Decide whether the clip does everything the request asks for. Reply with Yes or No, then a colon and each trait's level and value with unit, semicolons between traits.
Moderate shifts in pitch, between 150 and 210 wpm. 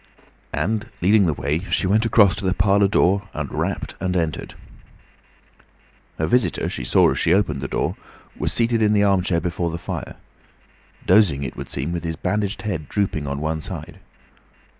Yes: average, 4.2 semitones; average, 180 wpm